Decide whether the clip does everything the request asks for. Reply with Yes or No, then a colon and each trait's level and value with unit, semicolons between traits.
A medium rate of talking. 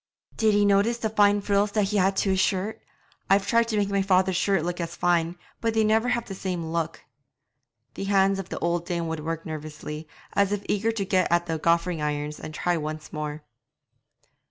No: fast, 210 wpm